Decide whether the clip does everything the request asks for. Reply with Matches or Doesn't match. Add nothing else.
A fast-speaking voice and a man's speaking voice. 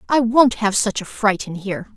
Doesn't match